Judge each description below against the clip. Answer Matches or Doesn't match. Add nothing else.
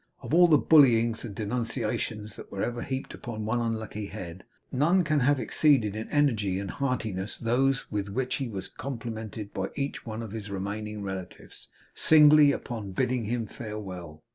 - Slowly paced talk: Doesn't match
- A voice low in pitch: Matches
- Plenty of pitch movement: Doesn't match